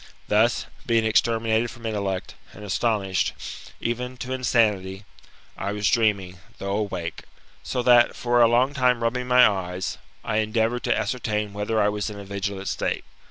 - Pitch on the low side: Yes, low, 110 Hz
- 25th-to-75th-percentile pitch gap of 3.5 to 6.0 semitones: No, average, 3.0 semitones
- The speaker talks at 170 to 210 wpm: No, average, 160 wpm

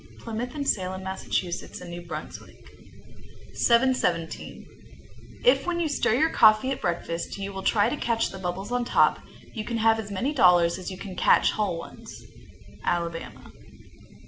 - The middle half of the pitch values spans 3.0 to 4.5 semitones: No, average, 5.2 semitones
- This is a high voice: Yes, high, 200 Hz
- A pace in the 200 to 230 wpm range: No, average, 160 wpm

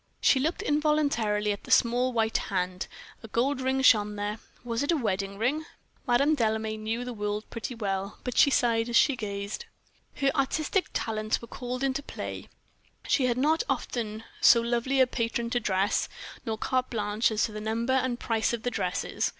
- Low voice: No, high, 235 Hz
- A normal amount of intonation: Yes, average, 3.4 semitones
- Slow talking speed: No, average, 185 wpm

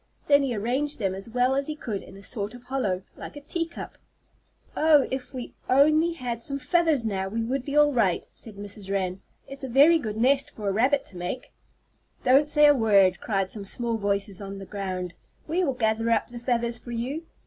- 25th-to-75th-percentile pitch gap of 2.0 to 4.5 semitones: No, wide, 5.6 semitones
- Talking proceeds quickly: Yes, fast, 215 wpm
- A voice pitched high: Yes, high, 240 Hz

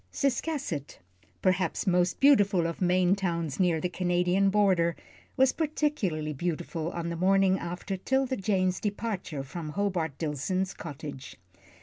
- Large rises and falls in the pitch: No, average, 2.9 semitones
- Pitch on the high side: No, medium, 180 Hz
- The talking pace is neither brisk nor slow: No, slow, 125 wpm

